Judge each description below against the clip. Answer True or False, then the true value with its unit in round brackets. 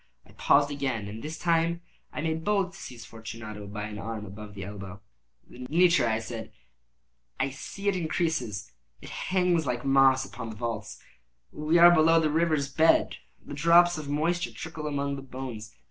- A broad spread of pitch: True (6.5 semitones)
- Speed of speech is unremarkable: True (175 wpm)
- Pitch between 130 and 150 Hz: True (140 Hz)